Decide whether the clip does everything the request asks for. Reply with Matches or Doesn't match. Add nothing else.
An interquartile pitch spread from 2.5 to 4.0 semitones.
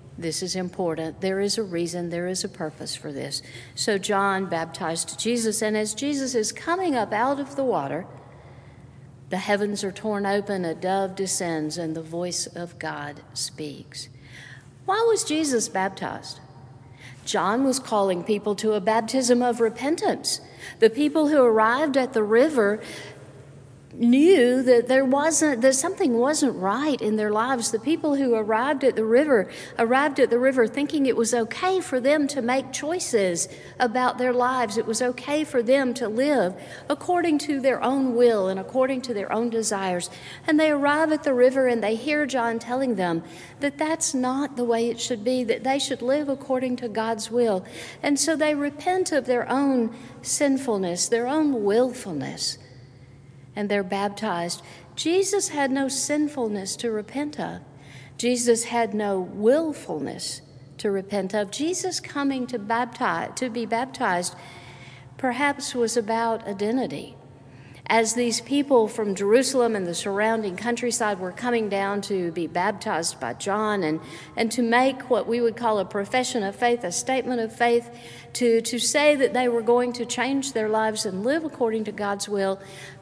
Doesn't match